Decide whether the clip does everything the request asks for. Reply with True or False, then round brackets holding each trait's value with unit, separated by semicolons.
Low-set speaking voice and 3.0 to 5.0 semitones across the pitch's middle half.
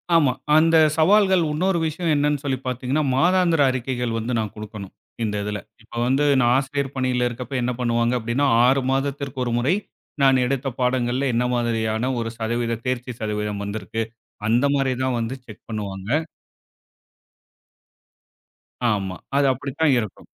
True (125 Hz; 3.6 semitones)